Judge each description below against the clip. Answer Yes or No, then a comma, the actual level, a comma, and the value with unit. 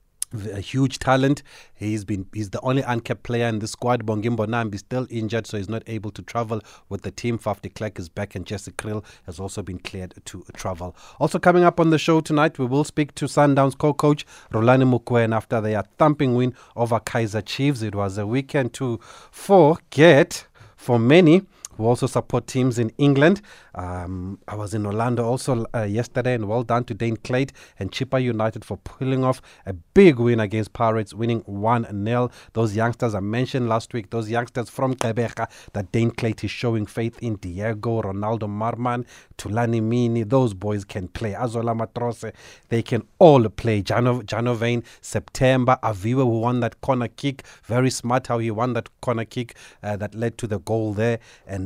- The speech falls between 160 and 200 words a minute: Yes, average, 185 wpm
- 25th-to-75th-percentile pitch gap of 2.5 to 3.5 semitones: Yes, average, 2.8 semitones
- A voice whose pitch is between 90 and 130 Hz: Yes, low, 115 Hz